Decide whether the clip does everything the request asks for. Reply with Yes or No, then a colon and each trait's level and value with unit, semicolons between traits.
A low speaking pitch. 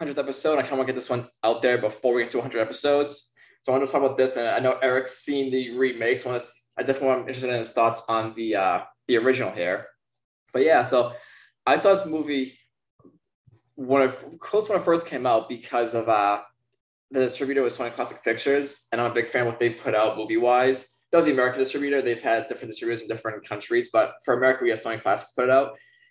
Yes: low, 130 Hz